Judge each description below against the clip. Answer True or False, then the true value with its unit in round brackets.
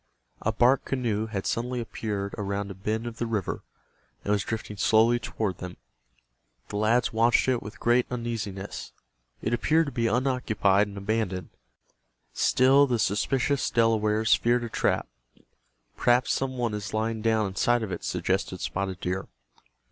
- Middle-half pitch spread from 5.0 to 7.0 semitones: False (2.8 semitones)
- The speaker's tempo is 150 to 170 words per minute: True (155 wpm)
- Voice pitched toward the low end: True (110 Hz)